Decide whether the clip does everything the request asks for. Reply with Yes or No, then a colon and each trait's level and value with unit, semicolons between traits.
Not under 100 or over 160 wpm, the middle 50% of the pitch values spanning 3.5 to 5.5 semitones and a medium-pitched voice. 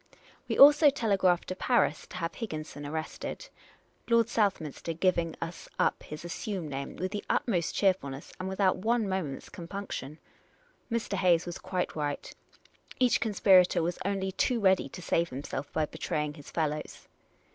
Yes: average, 150 wpm; average, 4.3 semitones; medium, 180 Hz